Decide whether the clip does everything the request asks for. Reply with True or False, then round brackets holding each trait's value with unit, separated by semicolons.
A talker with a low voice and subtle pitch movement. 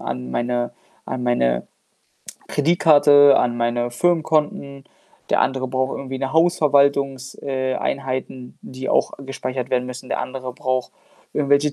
True (130 Hz; 2.0 semitones)